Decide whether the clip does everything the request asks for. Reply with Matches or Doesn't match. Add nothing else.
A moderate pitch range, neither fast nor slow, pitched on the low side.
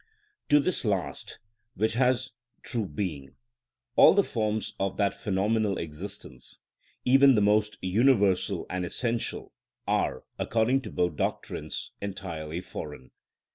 Doesn't match